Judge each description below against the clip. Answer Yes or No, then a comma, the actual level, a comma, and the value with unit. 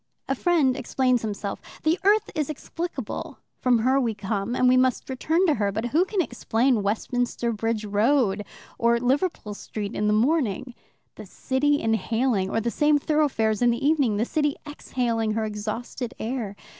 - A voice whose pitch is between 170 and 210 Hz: No, high, 245 Hz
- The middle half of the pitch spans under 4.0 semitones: No, average, 4.7 semitones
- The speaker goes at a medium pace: Yes, average, 170 wpm